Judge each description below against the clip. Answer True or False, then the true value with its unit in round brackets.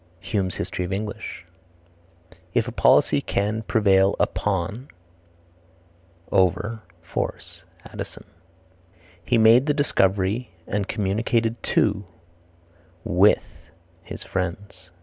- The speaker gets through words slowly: True (90 wpm)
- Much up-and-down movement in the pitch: False (2.7 semitones)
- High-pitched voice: False (100 Hz)